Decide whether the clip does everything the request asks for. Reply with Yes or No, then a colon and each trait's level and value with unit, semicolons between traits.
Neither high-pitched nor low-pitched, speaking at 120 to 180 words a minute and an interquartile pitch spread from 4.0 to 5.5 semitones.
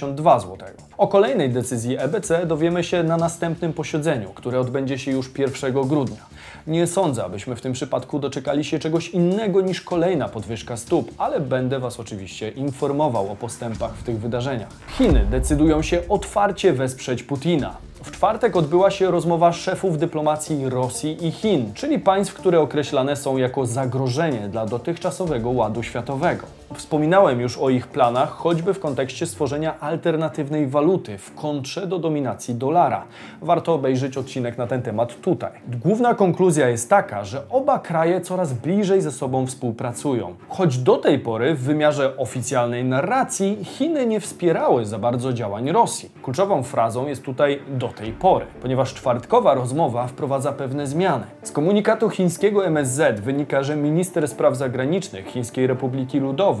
Yes: medium, 145 Hz; average, 150 wpm; average, 5.2 semitones